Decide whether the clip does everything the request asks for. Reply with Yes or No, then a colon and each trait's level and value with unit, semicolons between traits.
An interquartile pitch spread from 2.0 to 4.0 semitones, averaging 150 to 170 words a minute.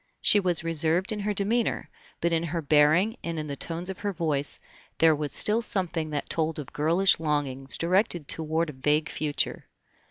No: average, 3.5 semitones; average, 185 wpm